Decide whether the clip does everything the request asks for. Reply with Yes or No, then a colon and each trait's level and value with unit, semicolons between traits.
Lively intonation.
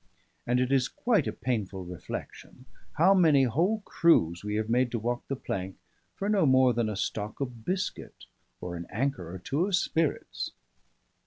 Yes: wide, 7.3 semitones